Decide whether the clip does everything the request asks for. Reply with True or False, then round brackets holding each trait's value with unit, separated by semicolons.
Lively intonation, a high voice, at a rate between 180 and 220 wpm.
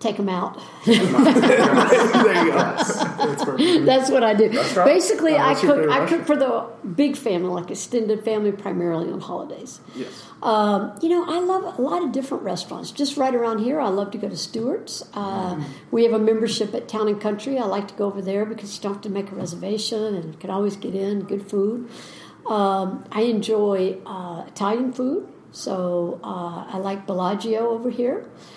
False (3.9 semitones; 215 Hz; 185 wpm)